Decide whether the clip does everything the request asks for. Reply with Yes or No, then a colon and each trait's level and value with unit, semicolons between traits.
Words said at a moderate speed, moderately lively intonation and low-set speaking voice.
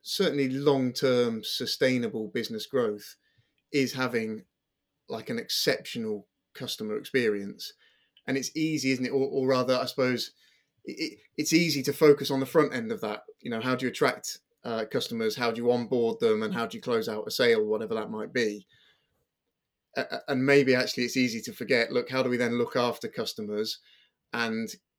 Yes: average, 185 wpm; average, 3.5 semitones; low, 130 Hz